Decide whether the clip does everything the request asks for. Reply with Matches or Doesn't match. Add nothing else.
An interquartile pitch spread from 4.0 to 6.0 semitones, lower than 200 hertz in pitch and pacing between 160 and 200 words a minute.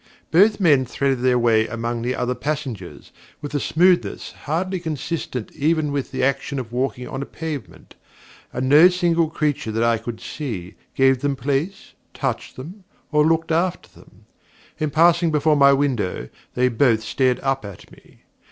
Matches